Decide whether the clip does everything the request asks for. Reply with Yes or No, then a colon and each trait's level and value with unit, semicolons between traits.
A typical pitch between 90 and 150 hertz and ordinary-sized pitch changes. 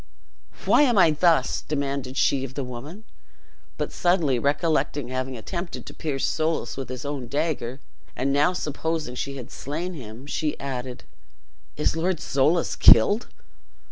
Yes: medium, 140 Hz; average, 3.8 semitones